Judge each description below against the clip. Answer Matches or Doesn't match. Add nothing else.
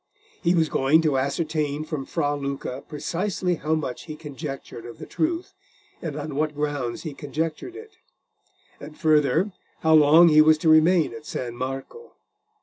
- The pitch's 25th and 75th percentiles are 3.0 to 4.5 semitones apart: Doesn't match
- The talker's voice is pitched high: Doesn't match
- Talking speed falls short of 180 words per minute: Matches